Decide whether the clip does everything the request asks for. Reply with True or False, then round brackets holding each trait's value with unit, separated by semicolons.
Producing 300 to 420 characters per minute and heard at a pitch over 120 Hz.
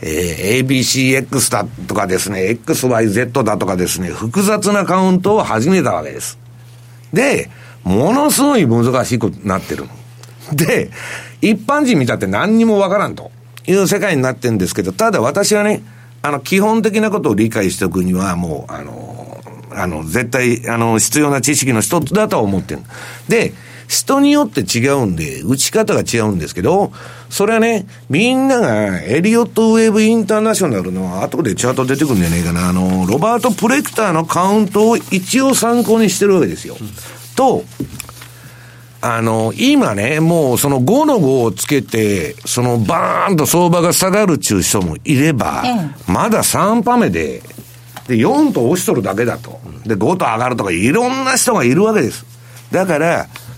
True (325 characters per minute; 135 Hz)